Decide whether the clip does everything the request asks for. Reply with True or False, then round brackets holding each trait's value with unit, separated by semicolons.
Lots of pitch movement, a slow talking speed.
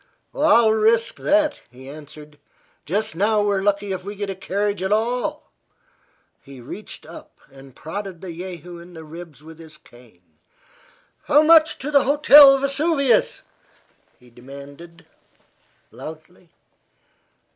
True (6.7 semitones; 130 wpm)